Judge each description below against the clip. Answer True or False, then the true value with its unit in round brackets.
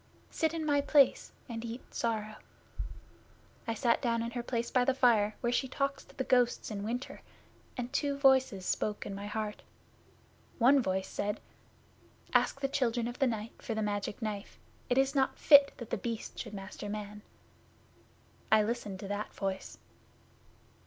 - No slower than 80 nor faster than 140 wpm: False (170 wpm)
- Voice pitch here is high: True (235 Hz)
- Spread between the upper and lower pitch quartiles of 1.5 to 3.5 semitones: False (3.9 semitones)